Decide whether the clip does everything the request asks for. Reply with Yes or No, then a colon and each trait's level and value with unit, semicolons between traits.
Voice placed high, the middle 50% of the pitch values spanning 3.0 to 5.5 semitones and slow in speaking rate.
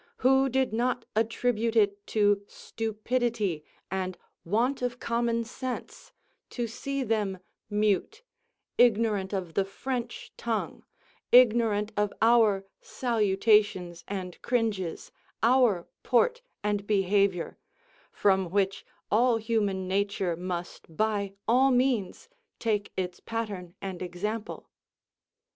Yes: high, 215 Hz; average, 3.4 semitones; slow, 105 wpm